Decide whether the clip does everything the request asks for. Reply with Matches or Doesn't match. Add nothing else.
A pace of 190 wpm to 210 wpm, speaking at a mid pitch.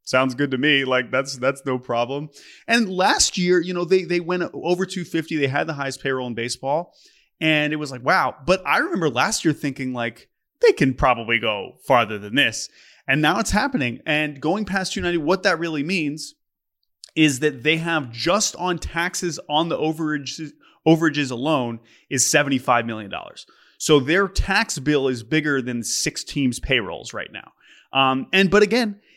Matches